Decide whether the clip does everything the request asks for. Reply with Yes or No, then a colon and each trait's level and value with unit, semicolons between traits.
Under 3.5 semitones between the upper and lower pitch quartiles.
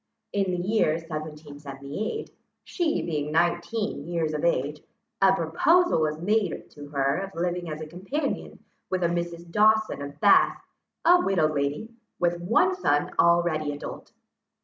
No: average, 4.3 semitones